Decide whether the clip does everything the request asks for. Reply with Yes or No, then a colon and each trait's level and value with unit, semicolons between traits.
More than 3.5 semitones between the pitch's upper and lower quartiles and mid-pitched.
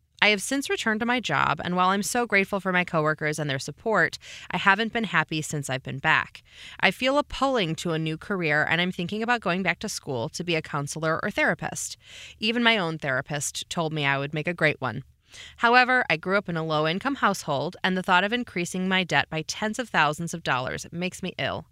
Yes: average, 4.8 semitones; medium, 175 Hz